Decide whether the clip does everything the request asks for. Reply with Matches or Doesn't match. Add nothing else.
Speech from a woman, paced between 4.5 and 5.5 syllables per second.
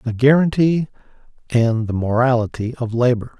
Doesn't match